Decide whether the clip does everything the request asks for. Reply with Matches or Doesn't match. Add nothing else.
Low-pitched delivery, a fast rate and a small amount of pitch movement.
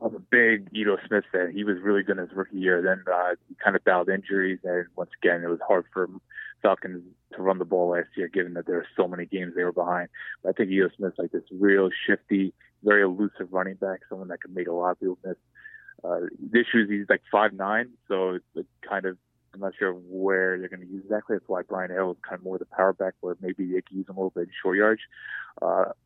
Matches